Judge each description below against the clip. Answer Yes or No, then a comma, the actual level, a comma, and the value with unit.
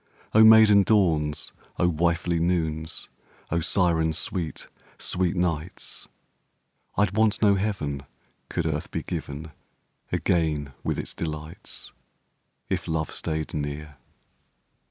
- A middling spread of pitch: Yes, average, 3.2 semitones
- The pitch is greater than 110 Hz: No, very low, 85 Hz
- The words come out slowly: Yes, slow, 110 wpm